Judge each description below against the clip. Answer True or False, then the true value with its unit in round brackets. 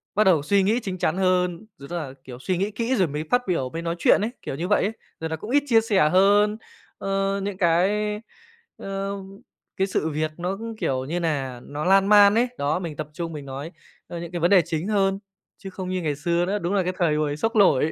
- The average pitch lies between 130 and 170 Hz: False (185 Hz)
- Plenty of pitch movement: False (4.1 semitones)